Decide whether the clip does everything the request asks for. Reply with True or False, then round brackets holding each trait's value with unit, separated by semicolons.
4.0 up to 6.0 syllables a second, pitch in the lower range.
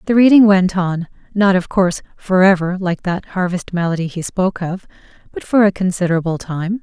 False (5.4 syllables/s; 185 Hz)